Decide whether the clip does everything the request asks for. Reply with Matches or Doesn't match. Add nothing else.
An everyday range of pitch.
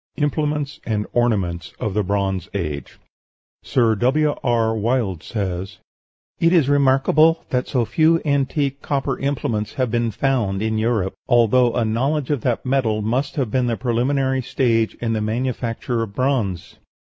Matches